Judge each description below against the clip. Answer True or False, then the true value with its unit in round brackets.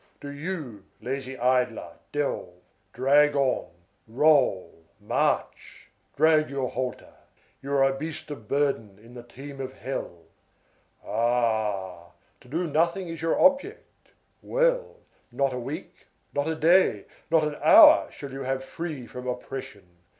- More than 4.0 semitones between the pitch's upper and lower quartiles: True (4.4 semitones)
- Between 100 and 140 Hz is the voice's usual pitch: True (135 Hz)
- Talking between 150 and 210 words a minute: False (135 wpm)